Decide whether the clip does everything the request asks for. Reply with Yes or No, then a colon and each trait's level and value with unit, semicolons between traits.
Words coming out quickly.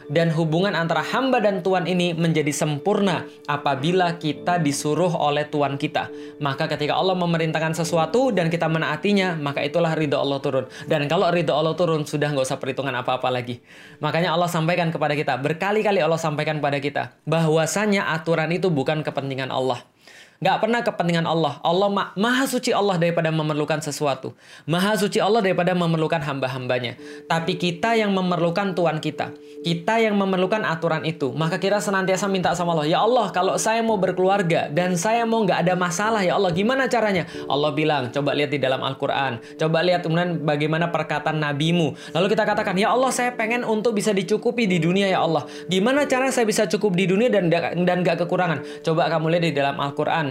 Yes: fast, 180 wpm